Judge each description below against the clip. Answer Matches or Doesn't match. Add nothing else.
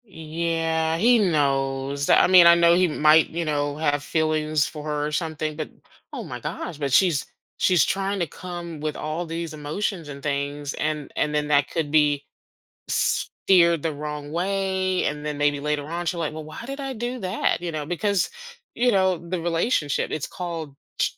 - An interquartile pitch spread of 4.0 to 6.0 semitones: Doesn't match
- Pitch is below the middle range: Doesn't match